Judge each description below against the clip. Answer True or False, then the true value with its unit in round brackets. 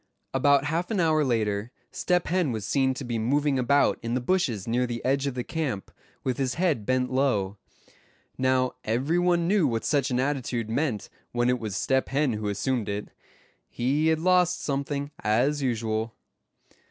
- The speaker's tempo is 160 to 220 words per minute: True (175 wpm)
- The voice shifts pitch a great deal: False (3.9 semitones)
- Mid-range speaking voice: False (130 Hz)